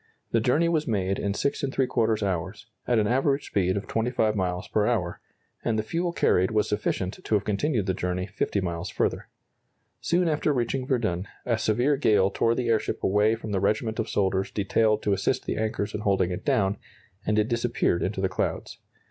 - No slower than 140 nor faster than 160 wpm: No, average, 190 wpm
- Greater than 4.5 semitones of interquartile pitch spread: No, average, 3.5 semitones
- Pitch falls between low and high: No, low, 105 Hz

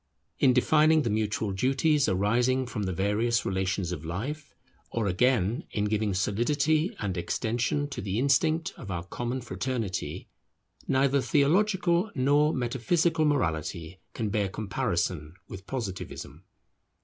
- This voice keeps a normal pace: No, slow, 125 wpm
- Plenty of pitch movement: Yes, wide, 6.4 semitones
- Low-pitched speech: Yes, low, 120 Hz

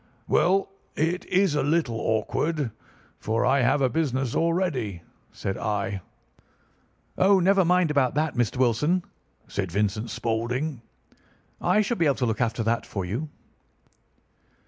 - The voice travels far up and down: Yes, wide, 6.6 semitones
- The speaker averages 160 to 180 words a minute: No, average, 140 wpm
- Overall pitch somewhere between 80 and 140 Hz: Yes, low, 135 Hz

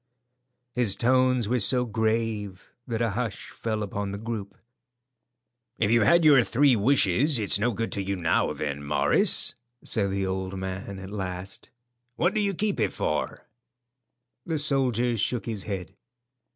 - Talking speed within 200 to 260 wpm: No, average, 155 wpm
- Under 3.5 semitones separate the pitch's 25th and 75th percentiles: No, average, 4.2 semitones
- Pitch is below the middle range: Yes, low, 110 Hz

